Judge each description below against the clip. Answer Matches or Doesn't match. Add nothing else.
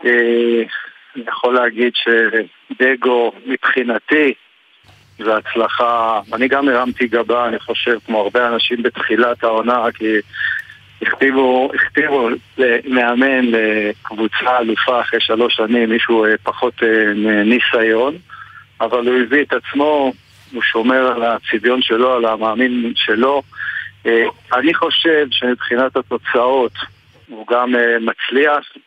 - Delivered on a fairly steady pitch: Matches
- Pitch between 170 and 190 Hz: Doesn't match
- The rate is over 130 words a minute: Doesn't match